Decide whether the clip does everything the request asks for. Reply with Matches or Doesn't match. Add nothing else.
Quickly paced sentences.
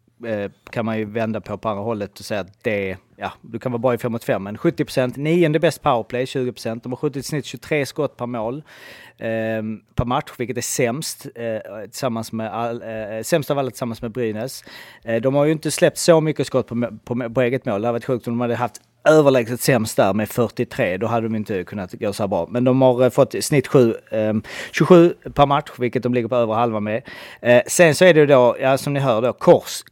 Matches